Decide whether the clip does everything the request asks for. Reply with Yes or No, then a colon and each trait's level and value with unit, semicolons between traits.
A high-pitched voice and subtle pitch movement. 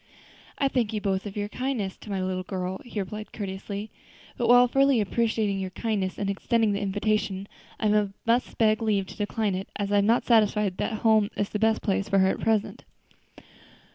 Yes: high, 210 Hz; narrow, 2.2 semitones